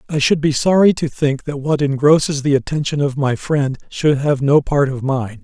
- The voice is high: No, medium, 140 Hz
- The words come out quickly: Yes, fast, 220 wpm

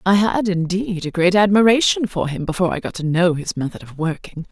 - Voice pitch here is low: No, medium, 185 Hz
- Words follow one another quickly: Yes, fast, 225 wpm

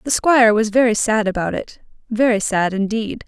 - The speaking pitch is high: Yes, high, 220 Hz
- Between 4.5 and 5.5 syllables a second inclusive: Yes, 5.3 syllables/s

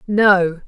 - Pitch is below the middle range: No, high, 190 Hz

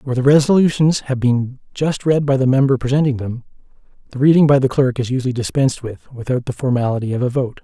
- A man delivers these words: Yes, male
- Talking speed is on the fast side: Yes, fast, 210 wpm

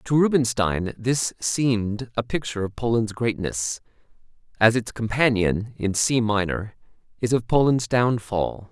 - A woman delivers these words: No, male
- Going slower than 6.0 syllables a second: Yes, 4.3 syllables/s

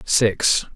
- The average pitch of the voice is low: Yes, low, 105 Hz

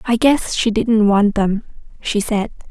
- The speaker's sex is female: Yes, female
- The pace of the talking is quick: No, average, 175 wpm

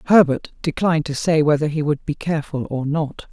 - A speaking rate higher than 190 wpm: Yes, average, 200 wpm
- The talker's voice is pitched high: No, medium, 155 Hz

